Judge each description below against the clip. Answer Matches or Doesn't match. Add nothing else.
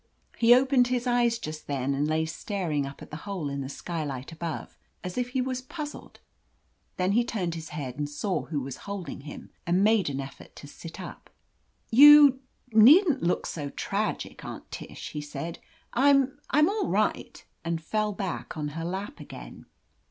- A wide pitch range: Matches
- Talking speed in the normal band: Matches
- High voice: Doesn't match